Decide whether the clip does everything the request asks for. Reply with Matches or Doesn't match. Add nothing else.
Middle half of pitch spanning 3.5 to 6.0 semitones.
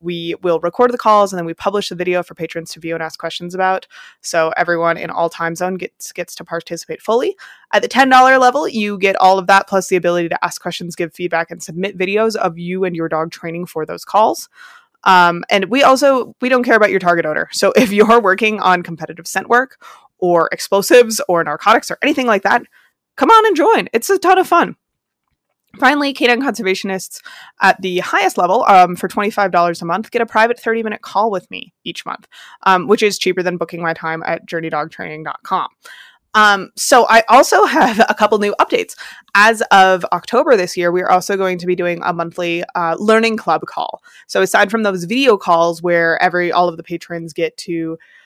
Matches